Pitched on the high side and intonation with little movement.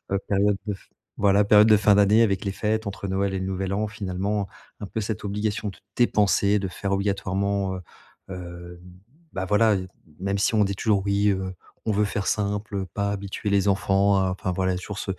No: low, 100 Hz; narrow, 1.2 semitones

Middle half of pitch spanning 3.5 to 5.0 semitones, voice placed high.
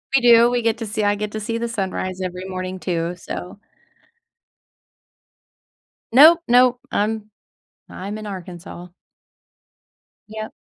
Yes: average, 3.8 semitones; high, 210 Hz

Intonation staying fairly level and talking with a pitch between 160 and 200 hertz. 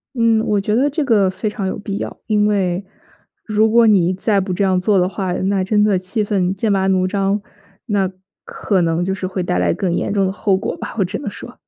Yes: narrow, 2.2 semitones; high, 195 Hz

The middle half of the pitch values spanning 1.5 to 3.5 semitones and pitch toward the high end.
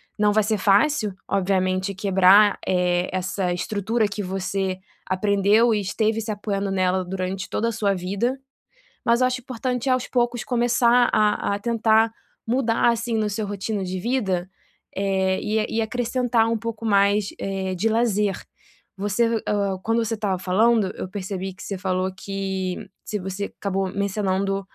Yes: average, 3.0 semitones; high, 200 Hz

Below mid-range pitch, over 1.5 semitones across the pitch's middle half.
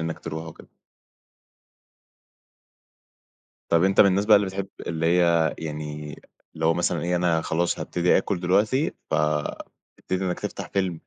Yes: very low, 85 Hz; average, 2.7 semitones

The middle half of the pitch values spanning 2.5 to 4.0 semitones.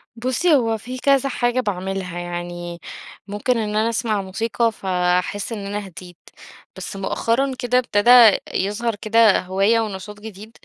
Yes: average, 3.4 semitones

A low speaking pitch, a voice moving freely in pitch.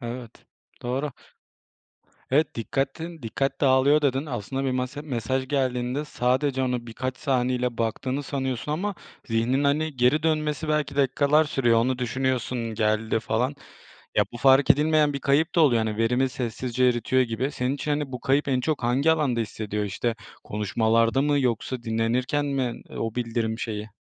No: low, 130 Hz; average, 3.3 semitones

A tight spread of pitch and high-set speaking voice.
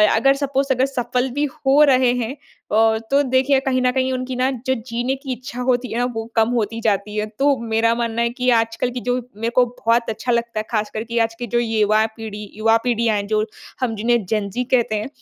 Yes: narrow, 2.3 semitones; high, 235 Hz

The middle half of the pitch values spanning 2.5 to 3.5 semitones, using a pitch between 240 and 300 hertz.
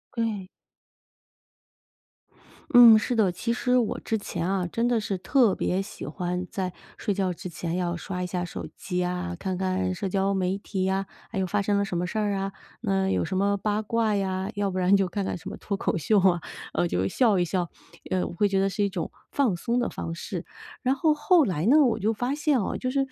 No: average, 3.2 semitones; high, 195 Hz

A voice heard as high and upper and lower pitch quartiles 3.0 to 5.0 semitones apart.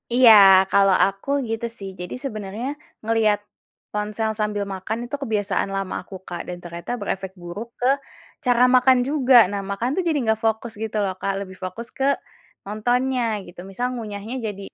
Yes: high, 215 Hz; average, 3.7 semitones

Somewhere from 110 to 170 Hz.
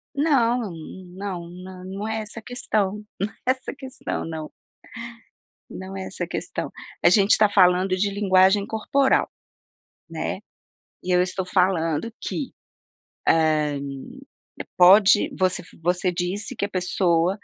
No: high, 190 Hz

